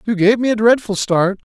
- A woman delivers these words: No, male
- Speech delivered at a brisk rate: Yes, fast, 240 wpm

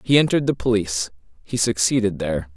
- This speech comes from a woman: No, male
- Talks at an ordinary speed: Yes, average, 165 wpm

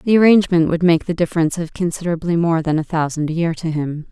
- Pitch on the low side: No, medium, 170 Hz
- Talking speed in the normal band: No, fast, 235 wpm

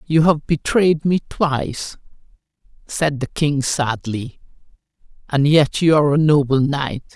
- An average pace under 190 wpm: Yes, slow, 135 wpm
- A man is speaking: No, female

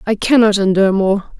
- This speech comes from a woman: Yes, female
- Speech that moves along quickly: No, average, 170 wpm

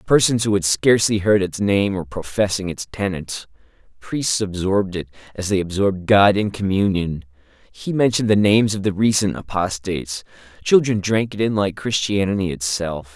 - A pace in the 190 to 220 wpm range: No, average, 150 wpm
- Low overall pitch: Yes, low, 100 Hz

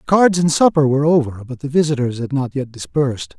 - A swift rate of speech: Yes, fast, 215 wpm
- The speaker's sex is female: No, male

